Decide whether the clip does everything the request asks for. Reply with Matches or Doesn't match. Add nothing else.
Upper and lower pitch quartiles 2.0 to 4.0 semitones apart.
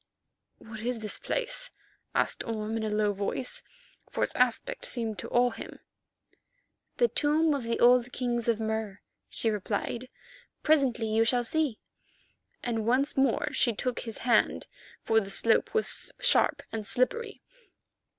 Matches